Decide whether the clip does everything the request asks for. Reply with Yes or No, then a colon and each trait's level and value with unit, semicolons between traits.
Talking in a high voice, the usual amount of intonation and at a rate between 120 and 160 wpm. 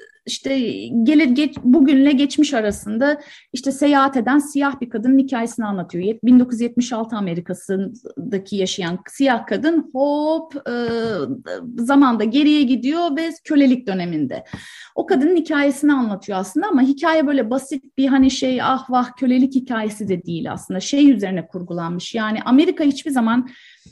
Yes: very high, 260 Hz; average, 4.5 semitones; average, 135 wpm